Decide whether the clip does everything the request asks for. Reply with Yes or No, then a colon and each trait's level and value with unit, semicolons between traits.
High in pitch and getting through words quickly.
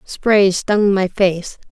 No: high, 195 Hz; average, 140 wpm